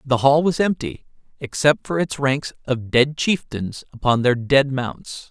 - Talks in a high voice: No, medium, 140 Hz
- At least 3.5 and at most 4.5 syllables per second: Yes, 4.1 syllables/s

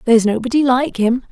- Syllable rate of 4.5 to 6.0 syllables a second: No, 6.3 syllables/s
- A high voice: Yes, high, 245 Hz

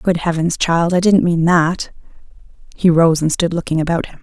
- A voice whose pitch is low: No, medium, 170 Hz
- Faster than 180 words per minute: Yes, average, 200 wpm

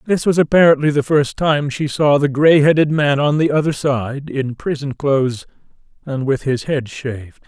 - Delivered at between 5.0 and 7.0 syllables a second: No, 4.7 syllables/s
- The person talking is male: Yes, male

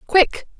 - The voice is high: Yes, very high, 375 Hz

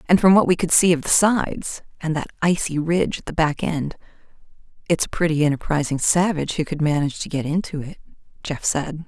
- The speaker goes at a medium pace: Yes, average, 190 wpm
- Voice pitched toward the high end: No, medium, 160 Hz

